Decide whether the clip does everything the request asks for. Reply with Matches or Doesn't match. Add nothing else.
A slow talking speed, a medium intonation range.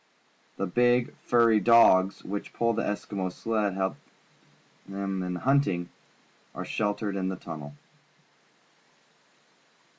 Matches